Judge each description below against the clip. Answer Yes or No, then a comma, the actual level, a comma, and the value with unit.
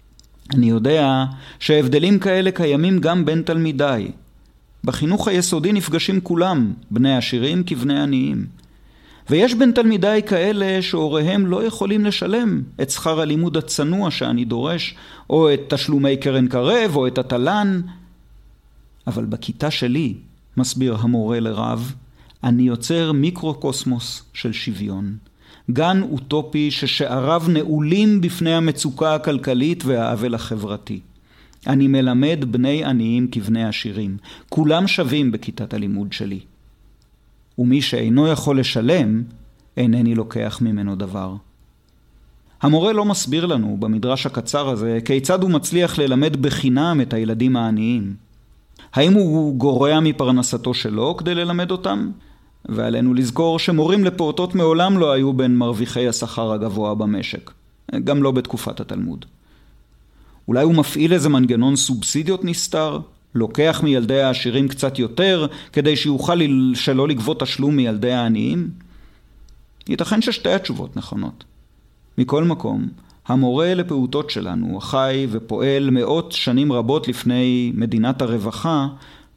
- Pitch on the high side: No, low, 135 Hz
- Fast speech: No, average, 115 wpm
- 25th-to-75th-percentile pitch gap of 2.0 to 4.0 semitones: No, wide, 5.4 semitones